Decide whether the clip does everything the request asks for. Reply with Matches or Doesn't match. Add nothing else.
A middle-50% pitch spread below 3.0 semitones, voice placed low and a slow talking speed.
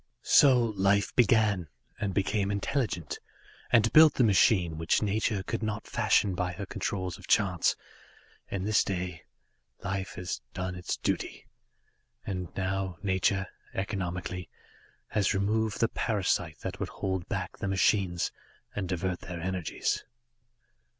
Matches